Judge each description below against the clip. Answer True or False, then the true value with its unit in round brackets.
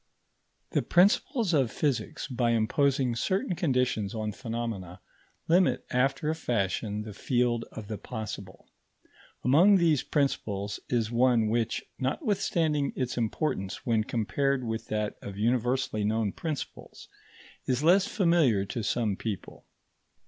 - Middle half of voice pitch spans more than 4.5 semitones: True (5.1 semitones)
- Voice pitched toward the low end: True (120 Hz)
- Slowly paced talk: True (125 wpm)